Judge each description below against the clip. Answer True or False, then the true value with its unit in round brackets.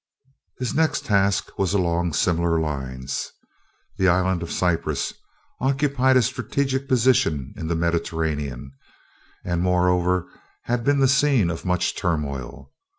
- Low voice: True (90 Hz)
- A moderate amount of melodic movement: False (7.5 semitones)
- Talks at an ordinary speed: False (125 wpm)